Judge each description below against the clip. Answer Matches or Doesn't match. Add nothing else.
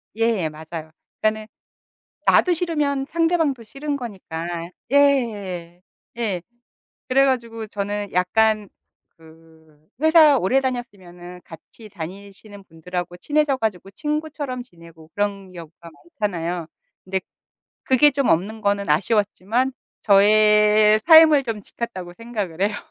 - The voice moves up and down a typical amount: Doesn't match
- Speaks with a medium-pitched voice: Doesn't match